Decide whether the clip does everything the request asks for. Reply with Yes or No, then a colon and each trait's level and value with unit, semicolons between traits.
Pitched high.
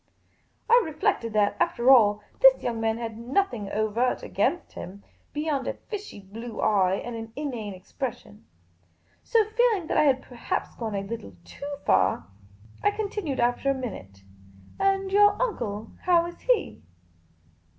Yes: high, 245 Hz